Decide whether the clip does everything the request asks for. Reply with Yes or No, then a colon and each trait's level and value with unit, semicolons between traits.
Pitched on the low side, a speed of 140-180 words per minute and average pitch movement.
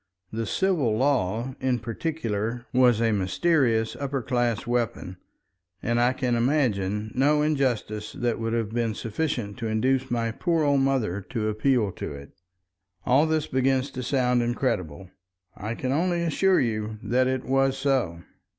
Yes: low, 120 Hz; average, 150 wpm; average, 3.5 semitones